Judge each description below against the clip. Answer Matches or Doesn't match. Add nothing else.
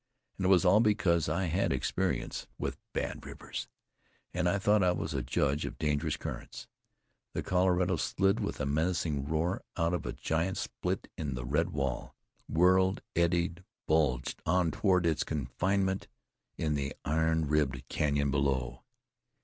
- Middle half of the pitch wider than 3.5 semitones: Matches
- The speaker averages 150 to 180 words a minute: Matches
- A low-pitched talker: Matches